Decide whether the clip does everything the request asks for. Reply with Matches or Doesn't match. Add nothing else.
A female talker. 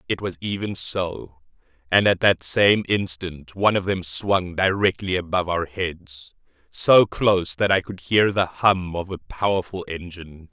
Doesn't match